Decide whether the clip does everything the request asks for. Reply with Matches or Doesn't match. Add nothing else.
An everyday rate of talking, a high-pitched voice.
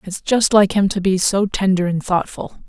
Doesn't match